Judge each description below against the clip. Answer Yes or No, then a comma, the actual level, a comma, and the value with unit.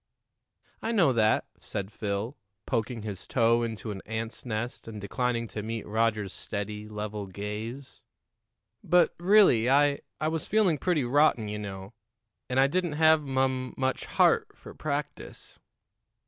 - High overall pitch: No, low, 115 Hz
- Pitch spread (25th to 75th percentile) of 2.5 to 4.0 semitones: No, average, 5.1 semitones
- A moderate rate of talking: Yes, average, 145 wpm